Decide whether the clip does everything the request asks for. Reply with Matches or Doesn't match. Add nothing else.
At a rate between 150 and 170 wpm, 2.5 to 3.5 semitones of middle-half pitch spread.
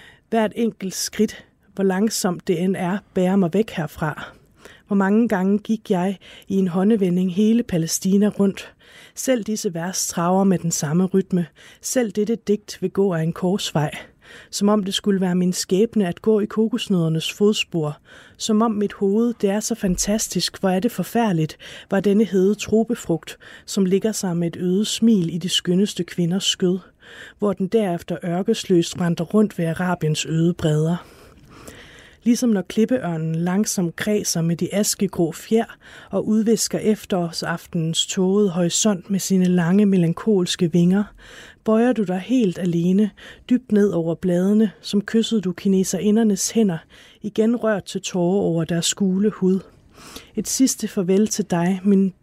Matches